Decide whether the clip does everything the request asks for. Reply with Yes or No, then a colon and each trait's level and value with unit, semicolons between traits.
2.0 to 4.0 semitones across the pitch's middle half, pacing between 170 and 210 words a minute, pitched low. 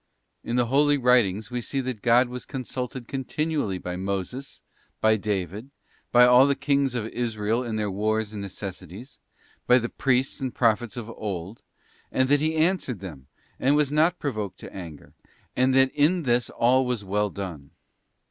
No: average, 4.4 semitones; average, 175 wpm; low, 120 Hz